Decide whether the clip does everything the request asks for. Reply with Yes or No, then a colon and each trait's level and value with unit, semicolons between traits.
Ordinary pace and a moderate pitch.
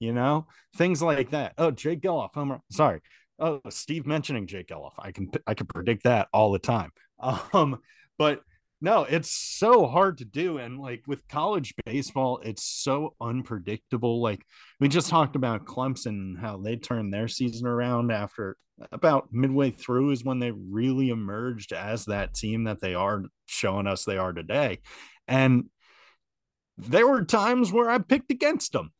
No: average, 165 wpm; low, 125 Hz